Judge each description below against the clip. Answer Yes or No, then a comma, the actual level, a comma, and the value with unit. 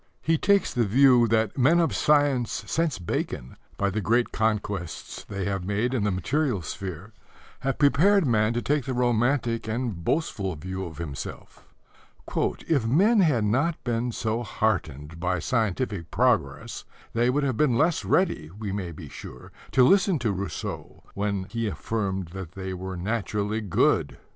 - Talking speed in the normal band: Yes, average, 160 wpm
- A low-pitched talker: Yes, low, 110 Hz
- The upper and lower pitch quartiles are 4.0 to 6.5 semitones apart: Yes, wide, 5.4 semitones